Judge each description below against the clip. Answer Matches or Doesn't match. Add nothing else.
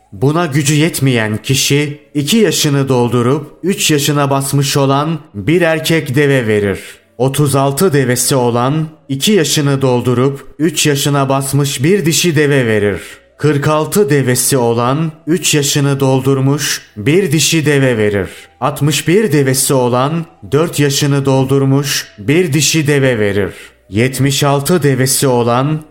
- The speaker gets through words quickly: Doesn't match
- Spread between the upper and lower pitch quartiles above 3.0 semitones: Doesn't match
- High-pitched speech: Doesn't match